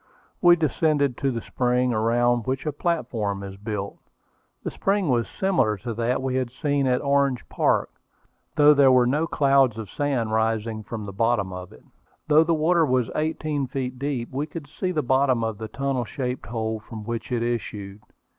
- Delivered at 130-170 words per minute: No, average, 190 wpm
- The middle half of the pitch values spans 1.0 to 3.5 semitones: No, average, 4.2 semitones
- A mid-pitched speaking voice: No, low, 125 Hz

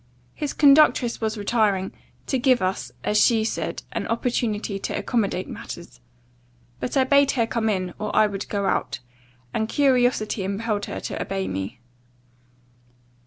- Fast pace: No, average, 150 wpm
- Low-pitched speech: No, high, 220 Hz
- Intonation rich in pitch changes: No, average, 3.8 semitones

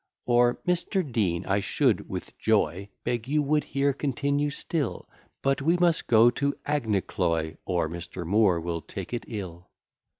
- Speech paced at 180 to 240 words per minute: No, average, 155 wpm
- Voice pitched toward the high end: No, low, 115 Hz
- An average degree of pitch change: No, wide, 7.9 semitones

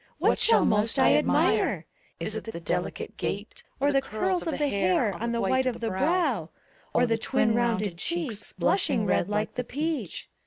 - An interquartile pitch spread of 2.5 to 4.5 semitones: No, average, 5.2 semitones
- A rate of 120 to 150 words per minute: No, average, 185 wpm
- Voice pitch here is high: Yes, high, 235 Hz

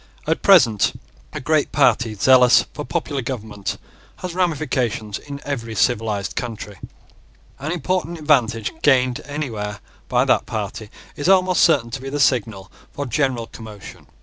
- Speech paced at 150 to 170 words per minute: No, average, 140 wpm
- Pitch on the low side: Yes, low, 125 Hz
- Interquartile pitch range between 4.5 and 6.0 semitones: Yes, average, 5.2 semitones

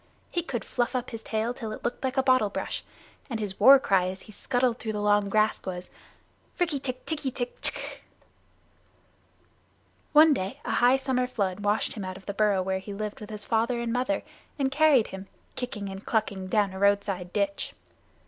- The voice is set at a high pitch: Yes, high, 220 Hz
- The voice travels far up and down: No, average, 4.2 semitones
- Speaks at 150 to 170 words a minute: No, average, 195 wpm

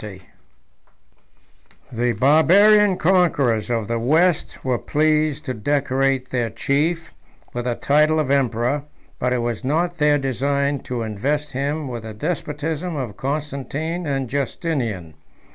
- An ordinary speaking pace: No, slow, 130 wpm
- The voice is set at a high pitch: No, medium, 140 Hz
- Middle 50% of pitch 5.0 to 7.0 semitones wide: No, average, 4.0 semitones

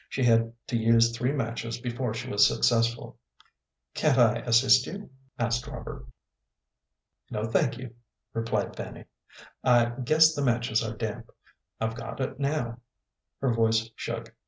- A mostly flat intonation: Yes, narrow, 1.9 semitones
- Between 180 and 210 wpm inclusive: No, average, 140 wpm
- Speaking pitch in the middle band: No, low, 115 Hz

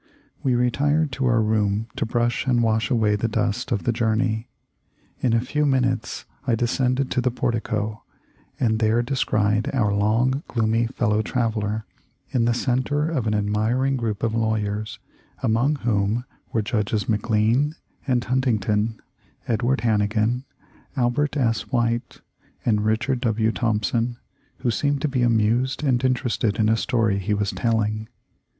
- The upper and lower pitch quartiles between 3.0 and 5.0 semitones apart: No, narrow, 2.6 semitones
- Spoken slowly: No, average, 145 wpm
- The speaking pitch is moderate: No, low, 115 Hz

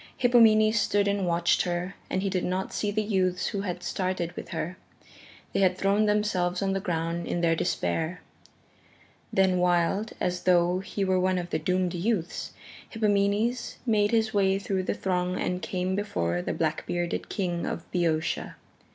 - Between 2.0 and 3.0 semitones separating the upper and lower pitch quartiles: Yes, narrow, 2.5 semitones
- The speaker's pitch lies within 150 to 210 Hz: Yes, medium, 185 Hz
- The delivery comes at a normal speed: Yes, average, 170 wpm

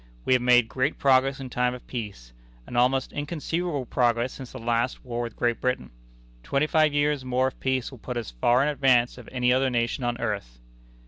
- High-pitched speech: No, low, 125 Hz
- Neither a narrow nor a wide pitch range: No, narrow, 2.0 semitones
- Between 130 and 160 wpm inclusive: No, fast, 205 wpm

